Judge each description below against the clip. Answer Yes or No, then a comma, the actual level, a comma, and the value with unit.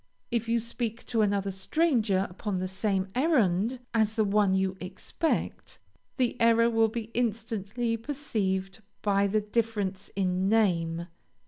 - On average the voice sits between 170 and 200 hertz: No, high, 215 Hz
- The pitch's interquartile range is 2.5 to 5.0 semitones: Yes, average, 3.3 semitones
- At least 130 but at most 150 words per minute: Yes, slow, 135 wpm